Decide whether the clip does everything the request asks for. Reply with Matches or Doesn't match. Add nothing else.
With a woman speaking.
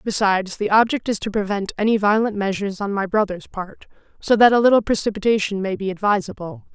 Matches